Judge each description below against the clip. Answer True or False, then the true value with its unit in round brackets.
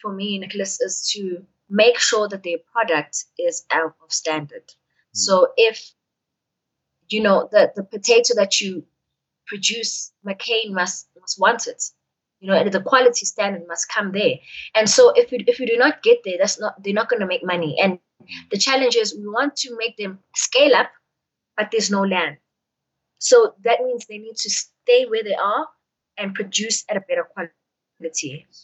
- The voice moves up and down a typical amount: True (4.5 semitones)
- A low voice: False (210 Hz)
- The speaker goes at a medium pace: True (180 wpm)